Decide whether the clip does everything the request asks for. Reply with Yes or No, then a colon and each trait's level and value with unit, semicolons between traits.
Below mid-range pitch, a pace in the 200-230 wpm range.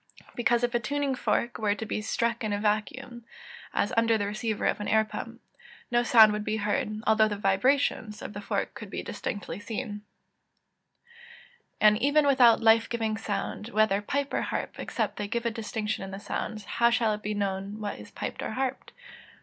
No: high, 220 Hz; fast, 205 wpm